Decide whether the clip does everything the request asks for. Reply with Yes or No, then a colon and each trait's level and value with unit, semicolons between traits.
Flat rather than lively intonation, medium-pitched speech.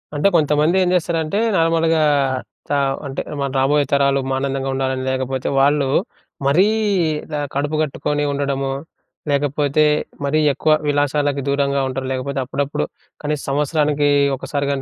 Yes: narrow, 1.6 semitones; medium, 145 Hz